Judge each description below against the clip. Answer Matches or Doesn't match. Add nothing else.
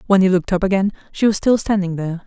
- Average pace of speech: Doesn't match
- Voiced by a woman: Matches